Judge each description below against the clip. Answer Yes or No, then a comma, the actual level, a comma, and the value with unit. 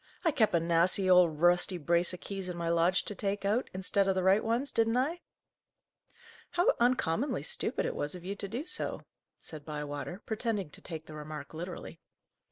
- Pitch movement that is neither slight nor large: Yes, average, 4.6 semitones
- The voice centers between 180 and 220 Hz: Yes, medium, 185 Hz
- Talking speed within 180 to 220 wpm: Yes, average, 190 wpm